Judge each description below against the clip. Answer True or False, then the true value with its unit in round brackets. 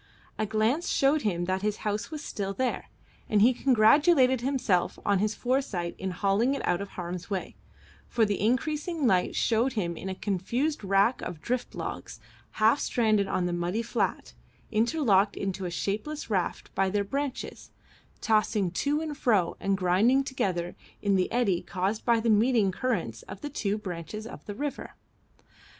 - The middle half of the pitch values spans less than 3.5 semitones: False (4.8 semitones)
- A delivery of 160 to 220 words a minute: True (165 wpm)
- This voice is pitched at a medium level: False (215 Hz)